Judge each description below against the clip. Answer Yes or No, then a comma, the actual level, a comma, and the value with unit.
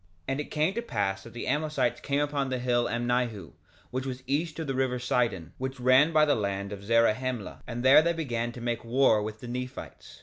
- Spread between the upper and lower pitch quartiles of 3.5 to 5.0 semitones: No, average, 3.1 semitones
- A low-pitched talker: Yes, low, 125 Hz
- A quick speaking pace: Yes, fast, 225 wpm